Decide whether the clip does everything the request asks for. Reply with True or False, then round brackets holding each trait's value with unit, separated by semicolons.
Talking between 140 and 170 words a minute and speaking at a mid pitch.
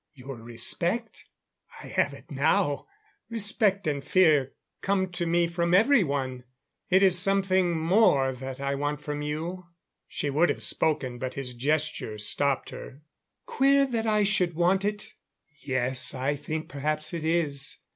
True (150 wpm; 160 Hz)